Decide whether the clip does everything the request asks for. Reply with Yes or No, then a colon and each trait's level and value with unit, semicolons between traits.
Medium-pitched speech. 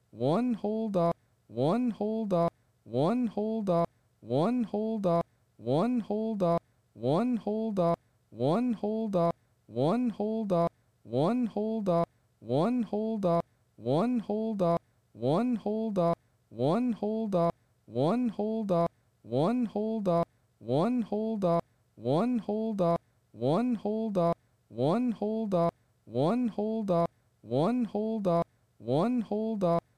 Yes: medium, 175 Hz